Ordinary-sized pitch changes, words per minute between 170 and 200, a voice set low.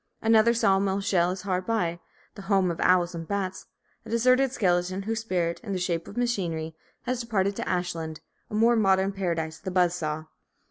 No: average, 3.8 semitones; average, 195 wpm; high, 190 Hz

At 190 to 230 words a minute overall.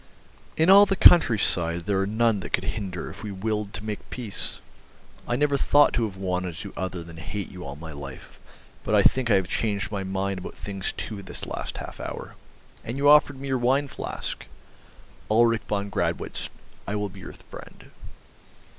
Yes: average, 195 wpm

